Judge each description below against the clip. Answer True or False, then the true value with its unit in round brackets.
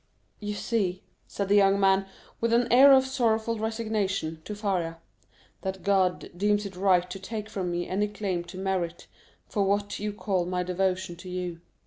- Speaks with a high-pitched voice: True (195 Hz)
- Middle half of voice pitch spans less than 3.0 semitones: True (2.5 semitones)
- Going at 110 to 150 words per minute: False (175 wpm)